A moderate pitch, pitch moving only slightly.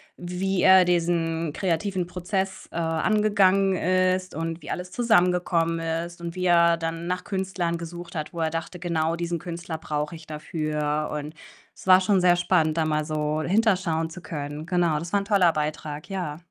Yes: medium, 170 Hz; narrow, 2.3 semitones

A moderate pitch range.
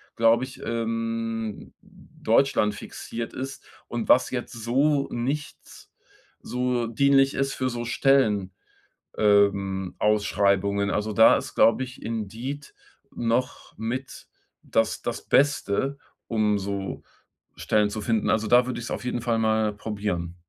Yes: average, 3.2 semitones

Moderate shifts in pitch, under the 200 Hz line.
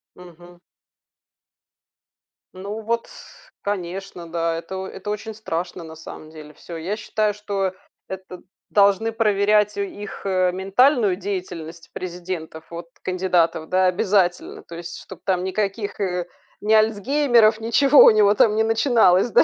Yes: average, 3.3 semitones; high, 190 Hz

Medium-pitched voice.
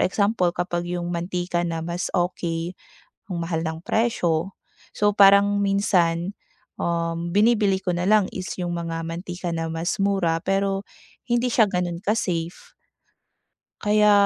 Yes: medium, 180 Hz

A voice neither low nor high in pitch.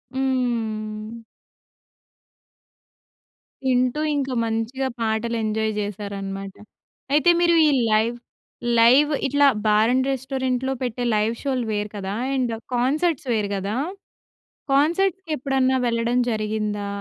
No: high, 240 Hz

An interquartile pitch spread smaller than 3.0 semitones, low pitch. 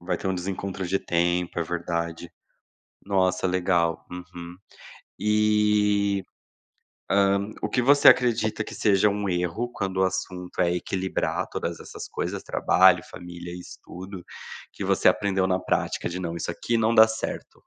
Yes: narrow, 2.6 semitones; very low, 95 Hz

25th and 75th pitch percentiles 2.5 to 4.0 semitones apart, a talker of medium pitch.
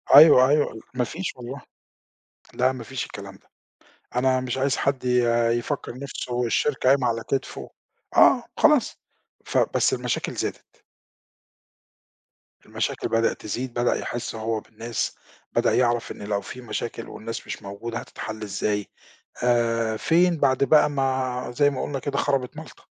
No: average, 2.8 semitones; low, 125 Hz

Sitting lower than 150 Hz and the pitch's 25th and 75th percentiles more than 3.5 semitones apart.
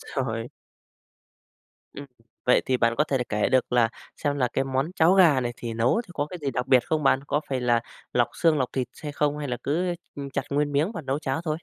No: low, 135 Hz; average, 3.2 semitones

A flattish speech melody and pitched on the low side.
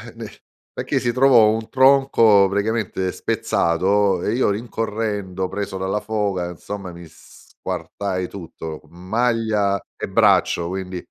No: average, 3.3 semitones; low, 100 Hz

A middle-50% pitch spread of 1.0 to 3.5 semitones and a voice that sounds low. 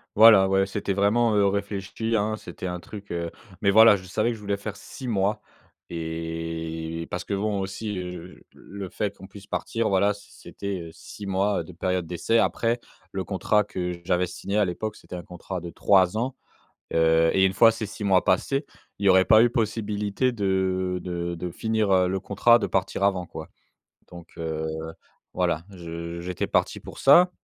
Yes: average, 2.9 semitones; very low, 95 Hz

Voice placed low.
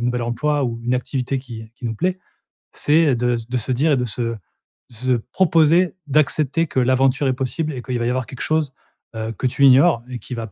Yes: low, 130 Hz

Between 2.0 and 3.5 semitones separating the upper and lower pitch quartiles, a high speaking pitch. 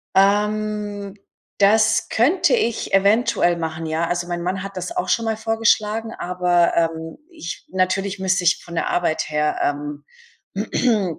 No: average, 4.0 semitones; high, 195 Hz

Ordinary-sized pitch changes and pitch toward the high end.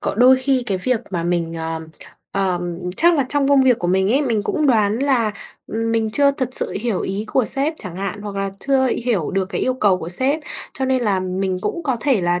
No: wide, 5.8 semitones; high, 220 Hz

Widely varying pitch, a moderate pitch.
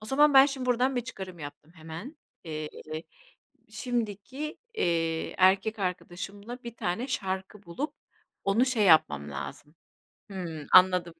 No: wide, 6.6 semitones; high, 195 Hz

